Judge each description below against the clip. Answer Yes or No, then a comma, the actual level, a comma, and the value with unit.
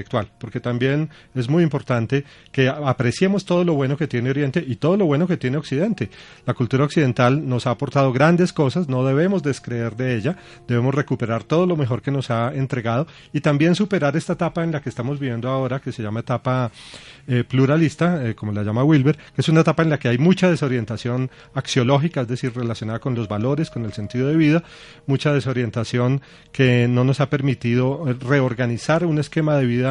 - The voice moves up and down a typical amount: Yes, average, 3.8 semitones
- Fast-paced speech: Yes, fast, 195 wpm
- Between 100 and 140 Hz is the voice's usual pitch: Yes, low, 135 Hz